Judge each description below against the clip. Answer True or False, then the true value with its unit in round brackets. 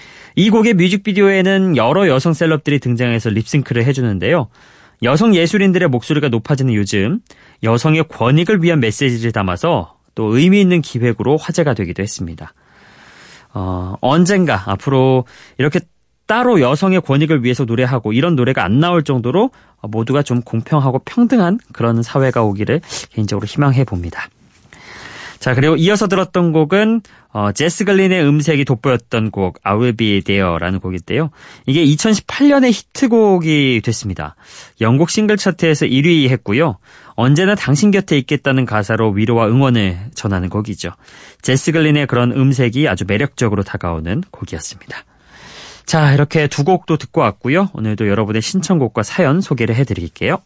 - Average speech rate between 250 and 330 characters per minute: False (355 characters per minute)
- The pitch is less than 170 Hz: True (135 Hz)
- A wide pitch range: True (7.0 semitones)